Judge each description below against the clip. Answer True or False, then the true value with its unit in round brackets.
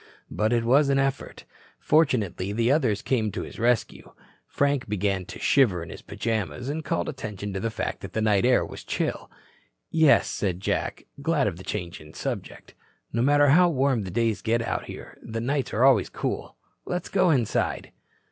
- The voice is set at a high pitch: False (115 Hz)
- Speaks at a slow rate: False (185 wpm)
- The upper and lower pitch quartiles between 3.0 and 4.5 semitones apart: False (5.2 semitones)